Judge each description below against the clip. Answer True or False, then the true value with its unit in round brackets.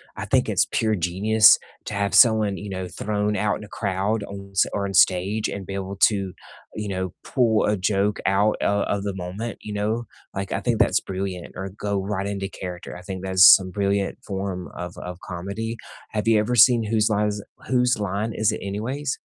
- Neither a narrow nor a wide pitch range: False (2.0 semitones)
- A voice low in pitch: True (100 Hz)